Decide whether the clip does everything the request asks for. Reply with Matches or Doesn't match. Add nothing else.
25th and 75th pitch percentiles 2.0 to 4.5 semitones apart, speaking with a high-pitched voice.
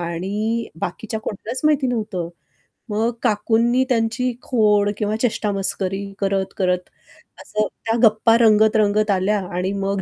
Matches